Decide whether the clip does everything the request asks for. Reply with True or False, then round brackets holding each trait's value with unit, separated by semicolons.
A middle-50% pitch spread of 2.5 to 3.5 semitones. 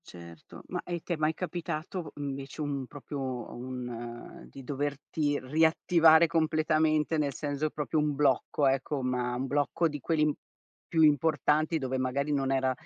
True (2.9 semitones)